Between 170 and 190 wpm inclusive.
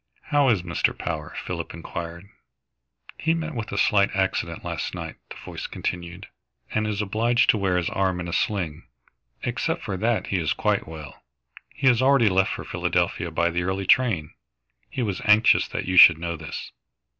Yes: average, 180 wpm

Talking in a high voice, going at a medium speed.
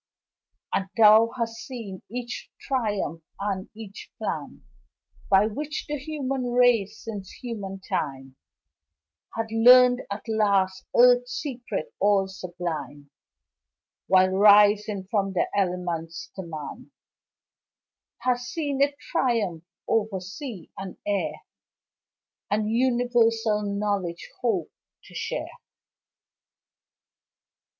No: high, 210 Hz; slow, 100 wpm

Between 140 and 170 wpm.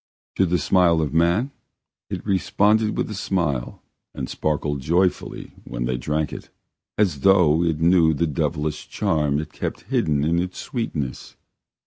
Yes: average, 150 wpm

